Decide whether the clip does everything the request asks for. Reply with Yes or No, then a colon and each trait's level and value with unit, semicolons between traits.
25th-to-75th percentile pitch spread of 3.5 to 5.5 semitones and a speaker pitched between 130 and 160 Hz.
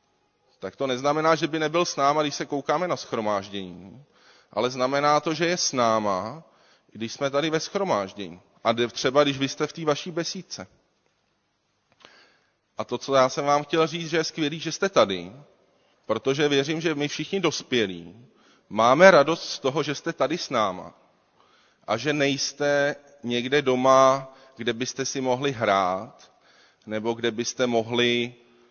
Yes: average, 4.4 semitones; medium, 140 Hz